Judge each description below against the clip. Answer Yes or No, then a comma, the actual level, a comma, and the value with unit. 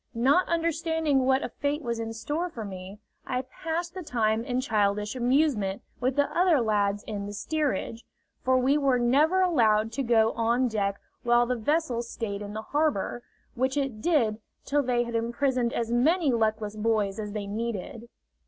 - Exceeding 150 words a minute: Yes, average, 175 wpm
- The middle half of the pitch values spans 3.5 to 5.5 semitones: Yes, average, 4.8 semitones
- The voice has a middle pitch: No, high, 240 Hz